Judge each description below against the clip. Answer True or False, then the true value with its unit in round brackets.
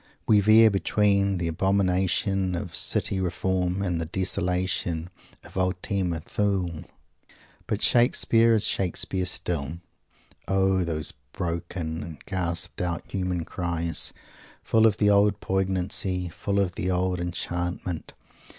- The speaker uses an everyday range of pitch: False (2.2 semitones)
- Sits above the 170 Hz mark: False (90 Hz)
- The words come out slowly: True (120 wpm)